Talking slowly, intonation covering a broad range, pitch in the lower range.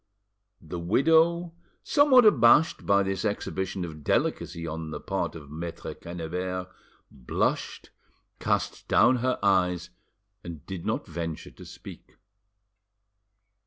Yes: slow, 115 wpm; wide, 6.1 semitones; very low, 90 Hz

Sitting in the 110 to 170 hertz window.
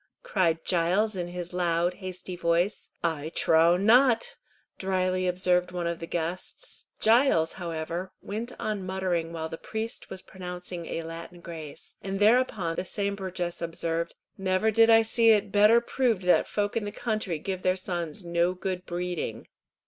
No: medium, 180 Hz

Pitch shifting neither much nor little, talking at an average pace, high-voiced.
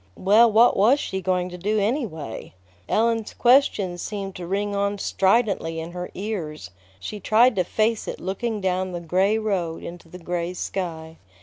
Yes: average, 3.6 semitones; average, 170 wpm; high, 195 Hz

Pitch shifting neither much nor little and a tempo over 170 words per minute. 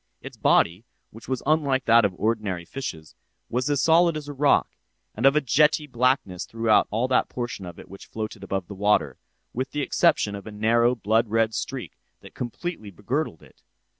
Yes: average, 4.8 semitones; average, 190 wpm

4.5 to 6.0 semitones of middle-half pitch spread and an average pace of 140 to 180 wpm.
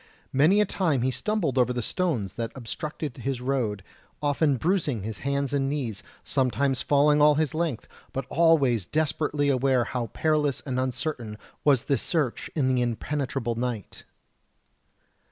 No: average, 3.5 semitones; average, 150 wpm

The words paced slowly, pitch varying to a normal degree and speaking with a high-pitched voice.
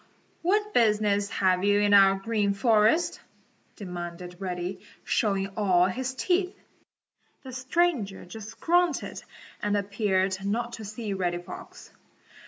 Yes: slow, 120 wpm; average, 3.7 semitones; high, 205 Hz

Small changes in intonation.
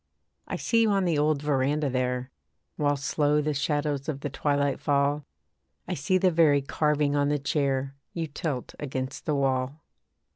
Yes: narrow, 1.6 semitones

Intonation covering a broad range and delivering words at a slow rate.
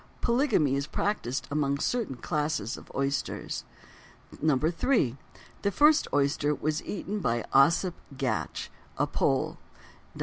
Yes: wide, 6.6 semitones; slow, 115 wpm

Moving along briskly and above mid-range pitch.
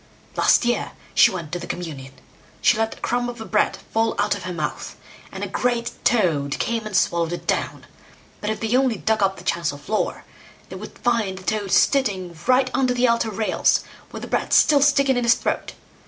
Yes: fast, 210 wpm; high, 220 Hz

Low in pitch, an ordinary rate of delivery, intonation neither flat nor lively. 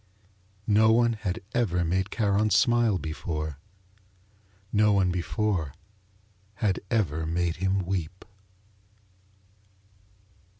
No: very low, 95 Hz; slow, 90 wpm; average, 3.9 semitones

